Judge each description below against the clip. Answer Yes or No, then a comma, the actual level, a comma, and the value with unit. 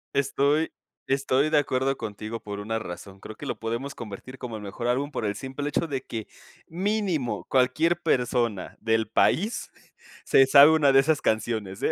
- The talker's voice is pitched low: Yes, low, 130 Hz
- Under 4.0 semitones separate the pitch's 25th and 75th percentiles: No, average, 4.4 semitones